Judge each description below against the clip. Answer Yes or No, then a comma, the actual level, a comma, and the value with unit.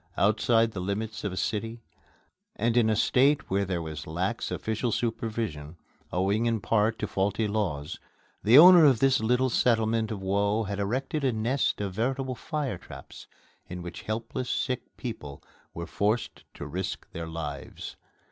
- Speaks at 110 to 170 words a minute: Yes, average, 160 wpm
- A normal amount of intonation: Yes, average, 3.6 semitones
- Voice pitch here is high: No, low, 110 Hz